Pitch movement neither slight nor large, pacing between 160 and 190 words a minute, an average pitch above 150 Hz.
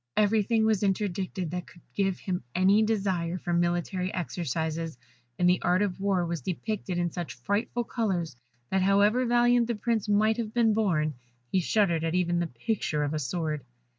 Yes: average, 3.7 semitones; average, 175 wpm; medium, 185 Hz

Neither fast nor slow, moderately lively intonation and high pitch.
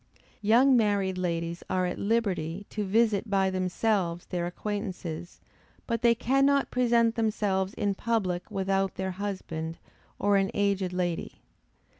No: slow, 130 wpm; average, 3.4 semitones; high, 195 Hz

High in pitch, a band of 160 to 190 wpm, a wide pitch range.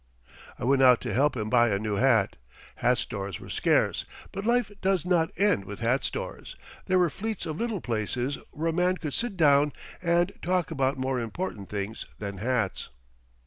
No: low, 135 Hz; average, 185 wpm; wide, 7.6 semitones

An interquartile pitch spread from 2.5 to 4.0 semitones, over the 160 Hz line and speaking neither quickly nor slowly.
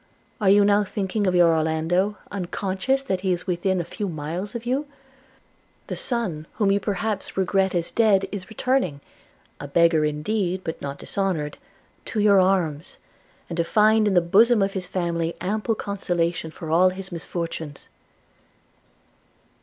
Yes: average, 3.4 semitones; high, 190 Hz; average, 160 wpm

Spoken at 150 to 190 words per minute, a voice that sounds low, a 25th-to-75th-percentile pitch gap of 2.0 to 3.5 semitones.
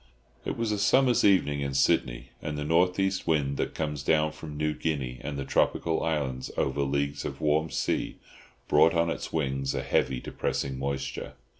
Yes: average, 180 wpm; very low, 75 Hz; average, 3.0 semitones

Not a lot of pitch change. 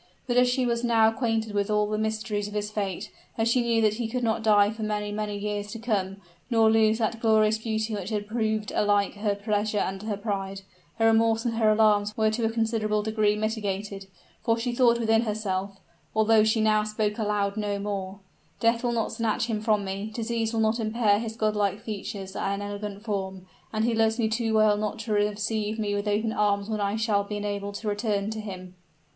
Yes: narrow, 1.5 semitones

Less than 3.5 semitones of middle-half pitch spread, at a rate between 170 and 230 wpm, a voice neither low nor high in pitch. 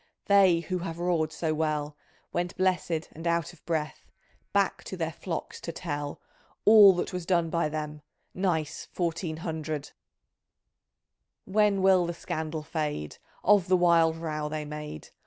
No: average, 2.7 semitones; average, 155 wpm; medium, 165 Hz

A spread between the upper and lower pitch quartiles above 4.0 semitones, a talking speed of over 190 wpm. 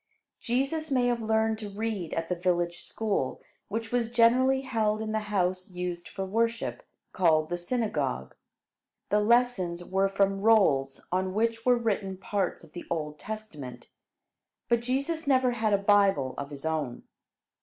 No: average, 4.8 semitones; average, 155 wpm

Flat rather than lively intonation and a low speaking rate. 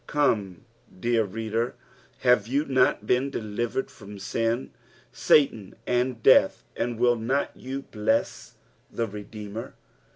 No: average, 3.0 semitones; slow, 120 wpm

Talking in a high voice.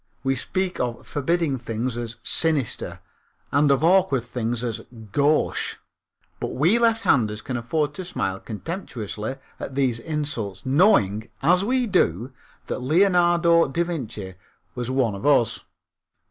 No: low, 135 Hz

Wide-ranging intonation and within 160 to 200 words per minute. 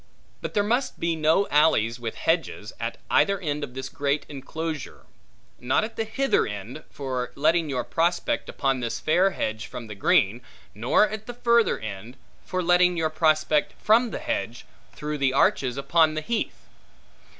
Yes: wide, 6.1 semitones; average, 170 wpm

